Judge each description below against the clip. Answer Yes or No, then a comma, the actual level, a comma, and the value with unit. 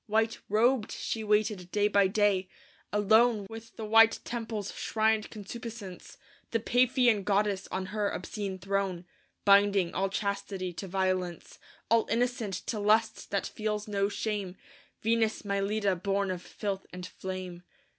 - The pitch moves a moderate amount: No, narrow, 2.3 semitones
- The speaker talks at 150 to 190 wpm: No, slow, 135 wpm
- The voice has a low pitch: No, high, 205 Hz